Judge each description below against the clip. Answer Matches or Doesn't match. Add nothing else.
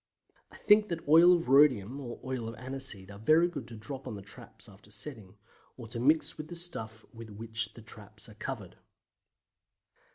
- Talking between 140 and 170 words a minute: Doesn't match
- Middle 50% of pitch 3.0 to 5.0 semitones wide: Doesn't match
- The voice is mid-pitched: Doesn't match